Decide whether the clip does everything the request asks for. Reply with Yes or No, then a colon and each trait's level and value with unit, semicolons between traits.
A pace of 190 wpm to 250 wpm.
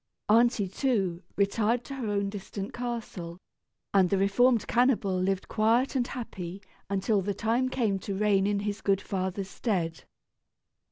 No: average, 150 wpm